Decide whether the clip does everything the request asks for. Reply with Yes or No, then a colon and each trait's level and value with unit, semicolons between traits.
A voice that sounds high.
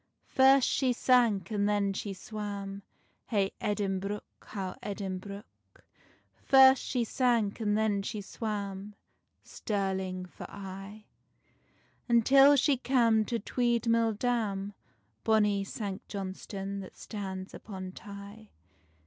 Yes: high, 205 Hz